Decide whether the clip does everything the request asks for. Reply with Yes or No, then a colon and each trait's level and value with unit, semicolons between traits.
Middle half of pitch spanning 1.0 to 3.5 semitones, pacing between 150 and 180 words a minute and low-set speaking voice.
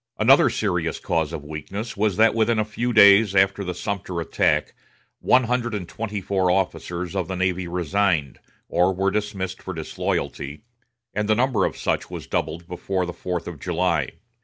Yes: average, 3.2 semitones; average, 175 wpm; very low, 95 Hz